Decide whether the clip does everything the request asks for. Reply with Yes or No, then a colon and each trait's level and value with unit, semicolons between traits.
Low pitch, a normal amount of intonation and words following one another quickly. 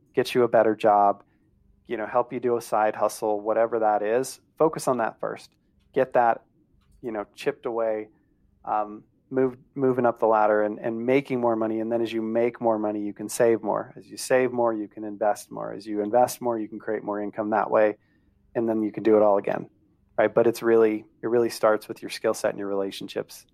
No: low, 110 Hz; narrow, 2.0 semitones; fast, 225 wpm